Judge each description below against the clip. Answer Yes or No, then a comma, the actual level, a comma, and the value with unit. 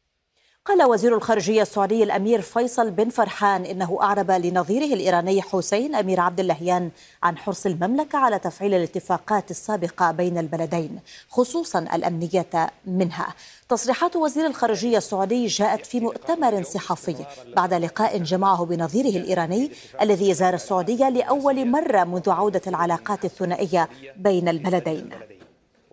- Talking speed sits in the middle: Yes, average, 120 wpm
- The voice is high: Yes, high, 195 Hz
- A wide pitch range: No, average, 4.0 semitones